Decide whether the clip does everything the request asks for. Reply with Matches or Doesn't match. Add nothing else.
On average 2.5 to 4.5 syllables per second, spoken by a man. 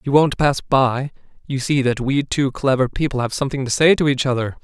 Doesn't match